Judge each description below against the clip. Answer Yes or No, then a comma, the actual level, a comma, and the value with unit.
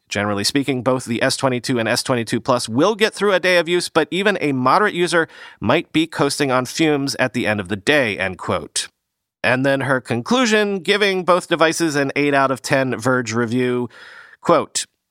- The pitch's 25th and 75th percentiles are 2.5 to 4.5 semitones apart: No, average, 5.1 semitones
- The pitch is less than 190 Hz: Yes, low, 135 Hz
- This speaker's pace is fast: No, average, 190 wpm